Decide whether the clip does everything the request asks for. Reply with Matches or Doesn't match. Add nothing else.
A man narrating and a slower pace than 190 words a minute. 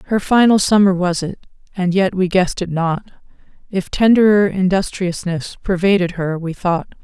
Doesn't match